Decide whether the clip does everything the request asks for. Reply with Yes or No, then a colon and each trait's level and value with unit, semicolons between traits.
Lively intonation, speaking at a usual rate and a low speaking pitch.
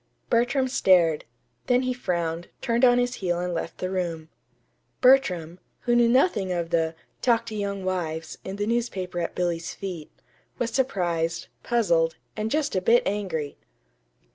No: wide, 5.9 semitones; average, 155 wpm; high, 190 Hz